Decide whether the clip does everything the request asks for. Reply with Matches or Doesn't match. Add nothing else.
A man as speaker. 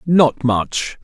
Matches